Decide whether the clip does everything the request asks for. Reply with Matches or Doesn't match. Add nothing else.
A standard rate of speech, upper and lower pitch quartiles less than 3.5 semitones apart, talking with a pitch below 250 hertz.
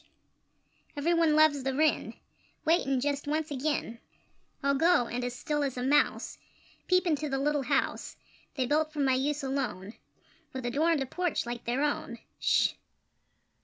Doesn't match